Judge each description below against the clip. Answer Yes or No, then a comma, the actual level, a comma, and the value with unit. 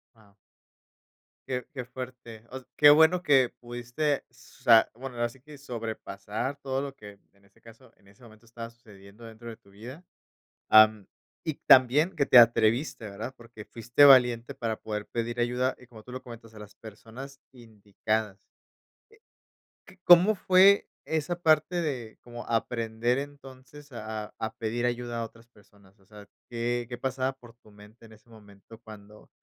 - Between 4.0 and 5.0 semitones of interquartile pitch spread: No, average, 3.2 semitones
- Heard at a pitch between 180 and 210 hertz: No, low, 120 Hz